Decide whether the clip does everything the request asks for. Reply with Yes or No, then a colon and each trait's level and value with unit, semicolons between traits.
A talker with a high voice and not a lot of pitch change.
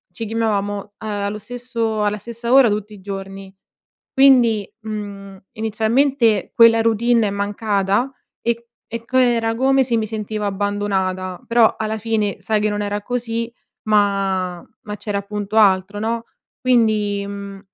Yes: high, 215 Hz; narrow, 2.3 semitones